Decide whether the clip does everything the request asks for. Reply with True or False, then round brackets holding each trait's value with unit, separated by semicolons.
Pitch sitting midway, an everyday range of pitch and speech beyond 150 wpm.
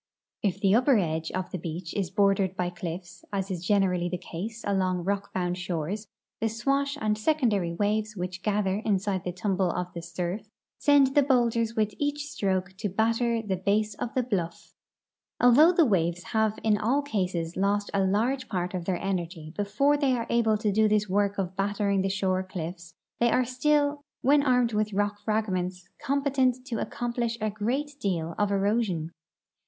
False (205 Hz; 4.1 semitones; 180 wpm)